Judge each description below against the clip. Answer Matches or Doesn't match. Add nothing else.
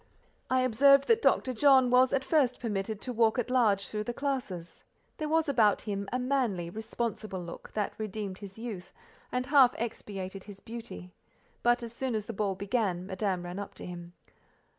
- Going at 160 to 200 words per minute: Matches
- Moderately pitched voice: Doesn't match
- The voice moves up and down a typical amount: Matches